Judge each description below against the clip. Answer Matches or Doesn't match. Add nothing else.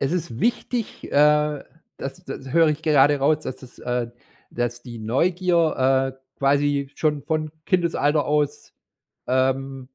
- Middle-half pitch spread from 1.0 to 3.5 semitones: Matches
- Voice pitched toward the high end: Doesn't match